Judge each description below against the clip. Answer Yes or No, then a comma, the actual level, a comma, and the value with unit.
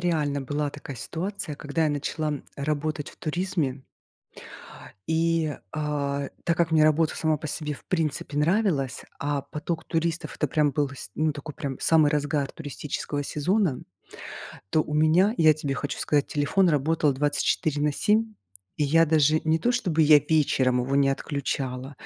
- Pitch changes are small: Yes, narrow, 2.1 semitones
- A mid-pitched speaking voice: Yes, medium, 150 Hz